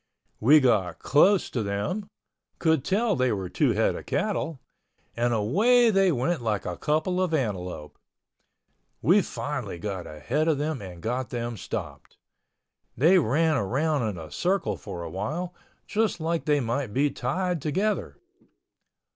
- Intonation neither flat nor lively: No, wide, 8.3 semitones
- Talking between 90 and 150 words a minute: Yes, average, 140 wpm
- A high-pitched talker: No, medium, 140 Hz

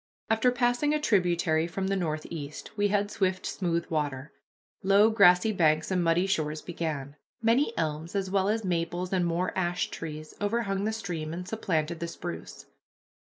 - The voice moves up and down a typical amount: Yes, average, 4.0 semitones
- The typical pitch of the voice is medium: Yes, medium, 180 Hz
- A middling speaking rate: Yes, average, 160 wpm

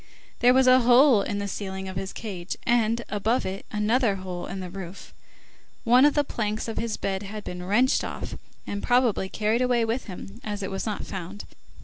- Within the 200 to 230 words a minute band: Yes, fast, 205 wpm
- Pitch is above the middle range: Yes, high, 210 Hz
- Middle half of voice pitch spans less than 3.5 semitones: No, average, 3.8 semitones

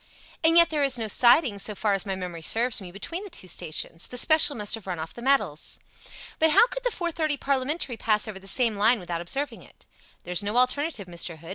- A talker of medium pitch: No, high, 230 Hz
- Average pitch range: No, wide, 7.3 semitones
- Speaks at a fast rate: Yes, fast, 235 wpm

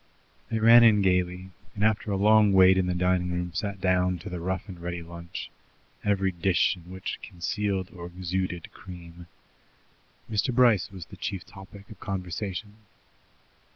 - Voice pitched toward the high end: No, very low, 95 Hz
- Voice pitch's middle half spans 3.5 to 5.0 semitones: No, narrow, 2.4 semitones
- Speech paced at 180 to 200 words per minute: No, average, 160 wpm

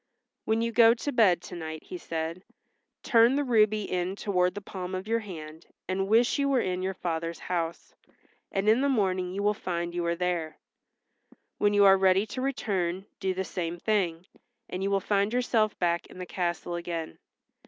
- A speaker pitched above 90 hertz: Yes, high, 190 Hz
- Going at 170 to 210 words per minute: Yes, average, 195 wpm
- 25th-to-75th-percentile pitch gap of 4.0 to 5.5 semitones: No, average, 3.6 semitones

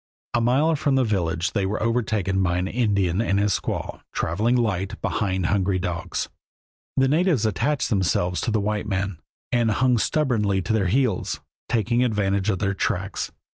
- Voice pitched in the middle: No, low, 105 Hz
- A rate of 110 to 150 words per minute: No, average, 170 wpm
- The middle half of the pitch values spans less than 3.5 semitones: No, average, 4.0 semitones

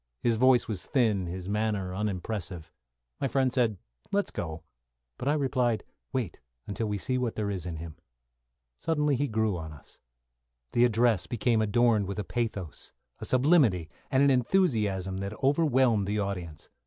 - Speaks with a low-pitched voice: Yes, low, 110 Hz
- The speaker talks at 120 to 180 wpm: Yes, average, 160 wpm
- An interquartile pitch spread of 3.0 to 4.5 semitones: No, average, 5.0 semitones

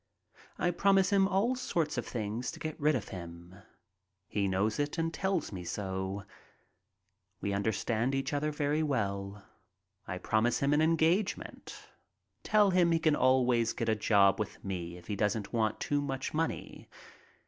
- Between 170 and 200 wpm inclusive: No, average, 160 wpm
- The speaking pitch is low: Yes, low, 130 Hz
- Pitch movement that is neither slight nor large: No, wide, 7.9 semitones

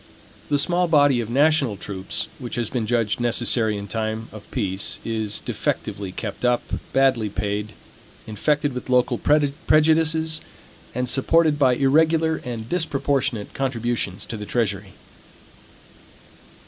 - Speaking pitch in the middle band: No, low, 125 Hz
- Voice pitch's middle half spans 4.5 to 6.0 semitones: Yes, average, 5.1 semitones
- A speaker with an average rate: No, slow, 125 wpm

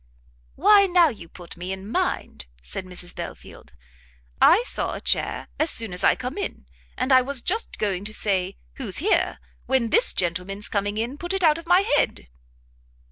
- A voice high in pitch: Yes, high, 235 Hz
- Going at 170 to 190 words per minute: Yes, average, 180 wpm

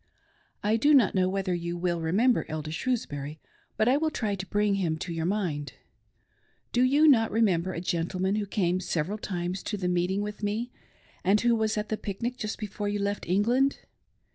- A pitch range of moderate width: Yes, average, 3.9 semitones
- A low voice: No, high, 200 Hz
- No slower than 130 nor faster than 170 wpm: No, average, 195 wpm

